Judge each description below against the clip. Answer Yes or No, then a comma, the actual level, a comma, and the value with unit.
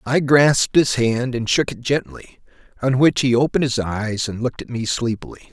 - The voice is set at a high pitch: No, low, 125 Hz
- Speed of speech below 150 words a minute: No, fast, 205 wpm